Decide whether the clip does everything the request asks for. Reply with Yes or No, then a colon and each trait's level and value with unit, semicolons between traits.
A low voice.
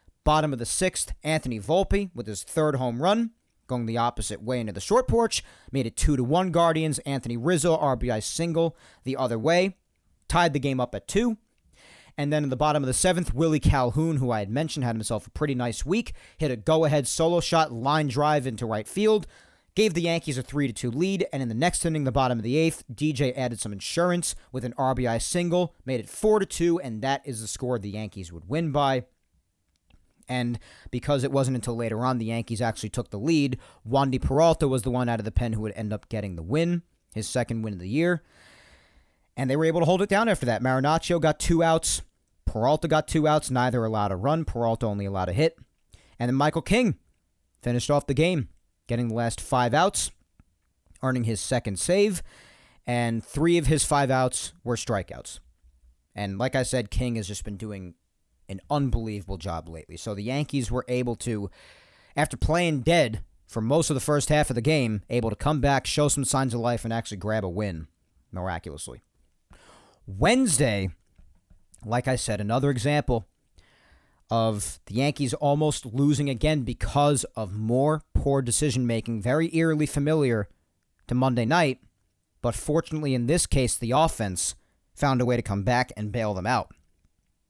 Yes: low, 125 Hz